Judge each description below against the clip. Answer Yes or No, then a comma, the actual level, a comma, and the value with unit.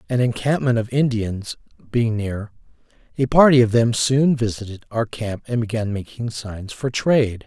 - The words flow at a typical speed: Yes, average, 160 wpm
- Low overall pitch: Yes, low, 115 Hz